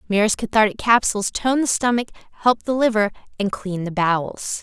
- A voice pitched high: Yes, high, 215 Hz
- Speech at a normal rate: Yes, average, 170 wpm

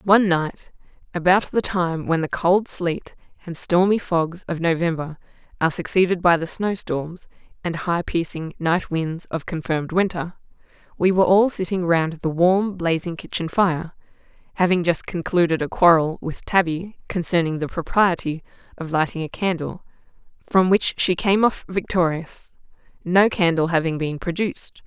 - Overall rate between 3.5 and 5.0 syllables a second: Yes, 4.7 syllables/s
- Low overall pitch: No, medium, 175 Hz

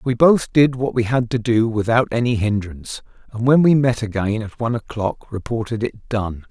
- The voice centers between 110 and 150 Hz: Yes, low, 115 Hz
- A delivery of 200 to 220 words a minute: Yes, fast, 205 wpm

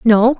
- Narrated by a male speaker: No, female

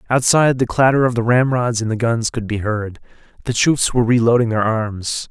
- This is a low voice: Yes, low, 120 Hz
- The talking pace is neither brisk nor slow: No, fast, 215 wpm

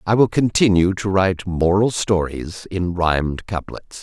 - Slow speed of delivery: No, average, 150 wpm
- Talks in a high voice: No, very low, 95 Hz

